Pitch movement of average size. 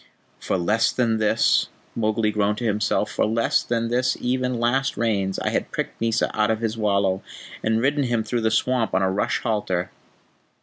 No: narrow, 2.2 semitones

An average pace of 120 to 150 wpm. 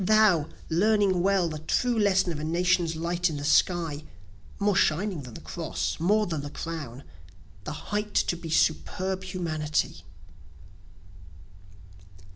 Yes: slow, 135 wpm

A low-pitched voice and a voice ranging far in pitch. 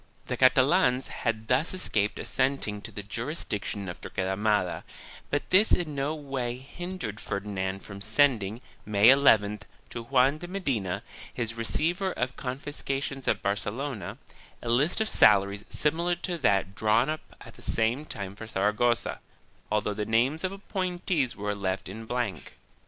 Yes: low, 120 Hz; wide, 5.8 semitones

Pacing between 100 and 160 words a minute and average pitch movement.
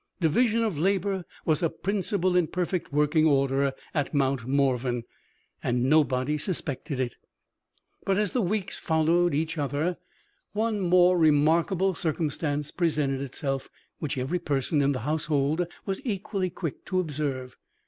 Yes: average, 140 wpm; average, 4.6 semitones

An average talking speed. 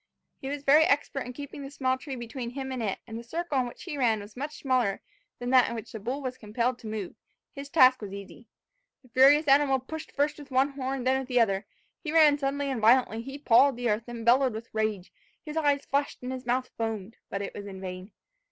No: fast, 245 wpm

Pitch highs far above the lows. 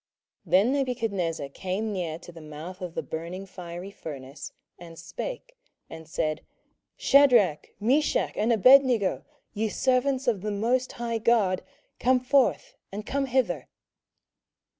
Yes: wide, 6.7 semitones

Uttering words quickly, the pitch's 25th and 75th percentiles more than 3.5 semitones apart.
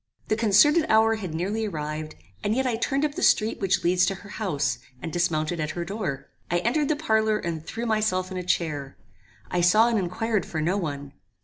Yes: fast, 210 wpm; average, 5.1 semitones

